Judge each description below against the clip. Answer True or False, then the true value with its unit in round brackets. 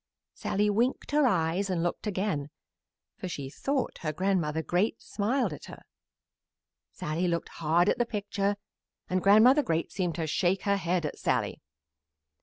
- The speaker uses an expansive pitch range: False (3.9 semitones)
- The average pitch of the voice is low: False (185 Hz)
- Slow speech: False (155 wpm)